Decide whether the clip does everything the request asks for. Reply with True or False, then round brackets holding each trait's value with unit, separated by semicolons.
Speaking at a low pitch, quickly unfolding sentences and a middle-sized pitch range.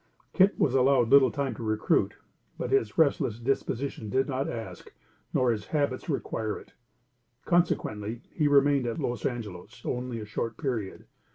False (125 Hz; 155 wpm; 3.8 semitones)